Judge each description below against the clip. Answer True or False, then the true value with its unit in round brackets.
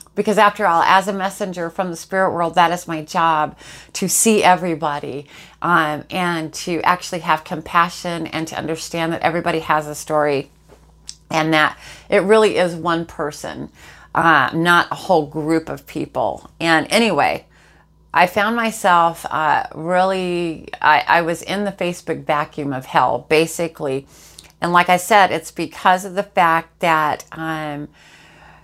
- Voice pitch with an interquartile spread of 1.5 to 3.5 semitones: True (2.7 semitones)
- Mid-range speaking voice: True (165 Hz)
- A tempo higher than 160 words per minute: False (155 wpm)